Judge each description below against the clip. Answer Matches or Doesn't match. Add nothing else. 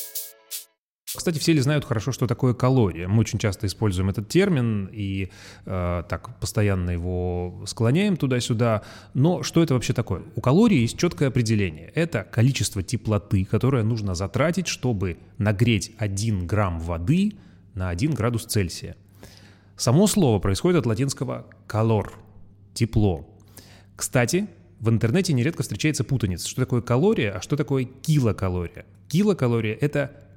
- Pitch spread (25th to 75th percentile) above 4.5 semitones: Matches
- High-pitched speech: Doesn't match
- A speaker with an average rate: Matches